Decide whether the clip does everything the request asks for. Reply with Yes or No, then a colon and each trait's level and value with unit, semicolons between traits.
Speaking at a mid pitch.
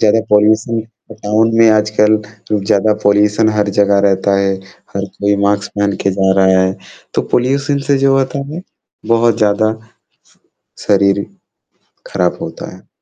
No: low, 105 Hz